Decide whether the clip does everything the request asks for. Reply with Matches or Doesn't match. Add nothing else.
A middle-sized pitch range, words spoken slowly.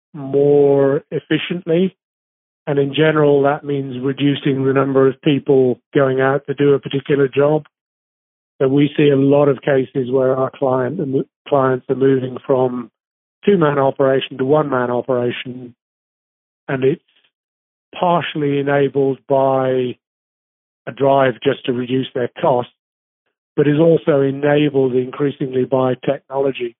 Doesn't match